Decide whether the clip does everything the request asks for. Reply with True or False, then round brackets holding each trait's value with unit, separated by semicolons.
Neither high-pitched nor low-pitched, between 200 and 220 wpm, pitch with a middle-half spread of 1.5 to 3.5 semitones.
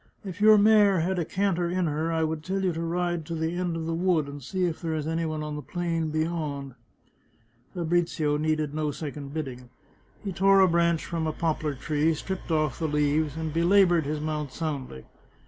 True (160 Hz; 205 wpm; 2.4 semitones)